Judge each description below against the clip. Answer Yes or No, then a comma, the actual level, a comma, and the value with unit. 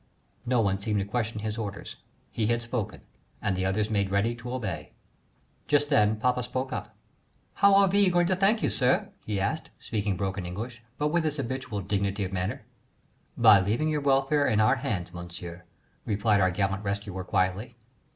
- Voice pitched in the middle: No, low, 110 Hz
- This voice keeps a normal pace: Yes, average, 180 wpm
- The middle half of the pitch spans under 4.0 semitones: No, average, 4.6 semitones